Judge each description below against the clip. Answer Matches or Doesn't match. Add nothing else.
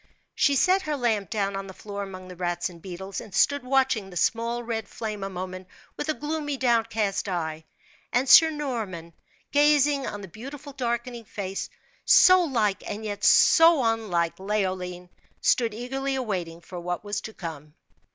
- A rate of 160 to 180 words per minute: Matches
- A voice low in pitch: Doesn't match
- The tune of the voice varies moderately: Doesn't match